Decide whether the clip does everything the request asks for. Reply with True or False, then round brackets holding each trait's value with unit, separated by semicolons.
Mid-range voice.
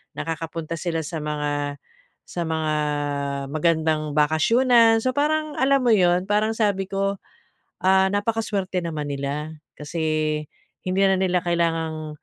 True (170 Hz)